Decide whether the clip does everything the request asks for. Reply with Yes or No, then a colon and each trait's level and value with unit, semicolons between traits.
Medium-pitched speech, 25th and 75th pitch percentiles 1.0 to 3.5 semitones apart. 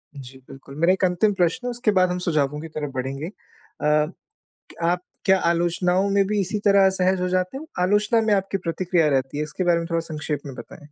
No: medium, 180 Hz; average, 4.1 semitones